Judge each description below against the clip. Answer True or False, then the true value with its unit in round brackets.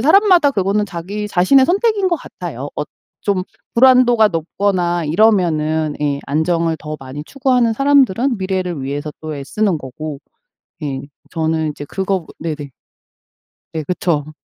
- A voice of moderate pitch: True (180 Hz)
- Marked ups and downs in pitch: True (6.6 semitones)